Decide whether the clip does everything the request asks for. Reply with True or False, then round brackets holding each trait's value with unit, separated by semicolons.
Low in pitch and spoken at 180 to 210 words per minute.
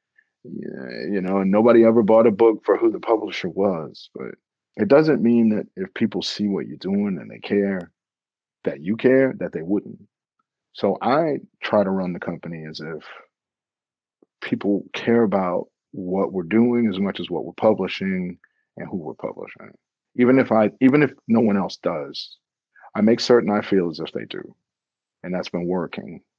True (110 Hz; 185 wpm)